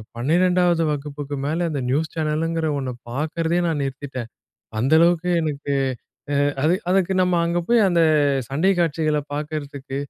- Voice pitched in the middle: Yes, medium, 155 Hz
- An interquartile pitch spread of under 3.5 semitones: Yes, average, 3.1 semitones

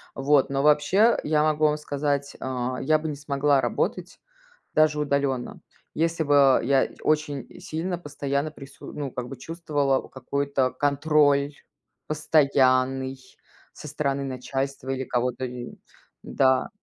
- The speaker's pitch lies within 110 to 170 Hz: Yes, medium, 140 Hz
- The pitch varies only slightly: Yes, narrow, 2.1 semitones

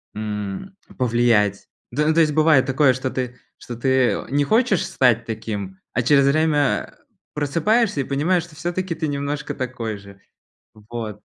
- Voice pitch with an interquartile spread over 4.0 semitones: Yes, average, 5.1 semitones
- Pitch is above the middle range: No, low, 135 Hz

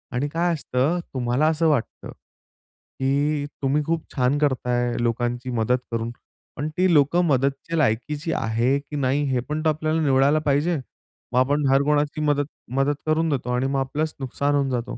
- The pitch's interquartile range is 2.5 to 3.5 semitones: Yes, average, 3.2 semitones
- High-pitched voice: No, medium, 140 Hz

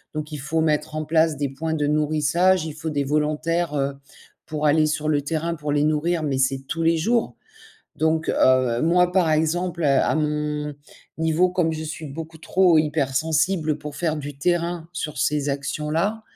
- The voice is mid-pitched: Yes, medium, 155 Hz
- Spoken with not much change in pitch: Yes, narrow, 1.8 semitones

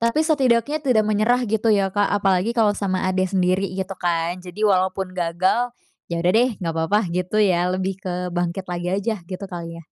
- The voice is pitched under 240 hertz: Yes, high, 190 Hz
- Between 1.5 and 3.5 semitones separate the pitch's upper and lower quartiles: Yes, average, 3.1 semitones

